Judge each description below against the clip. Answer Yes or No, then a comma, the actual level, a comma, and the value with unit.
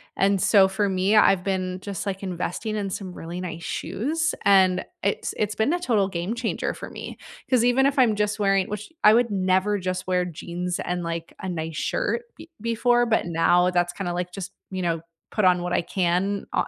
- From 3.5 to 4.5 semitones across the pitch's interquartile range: No, average, 3.0 semitones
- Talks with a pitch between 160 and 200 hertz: Yes, high, 190 Hz